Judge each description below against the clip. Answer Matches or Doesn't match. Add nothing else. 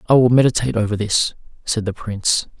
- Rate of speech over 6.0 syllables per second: Matches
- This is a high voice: Doesn't match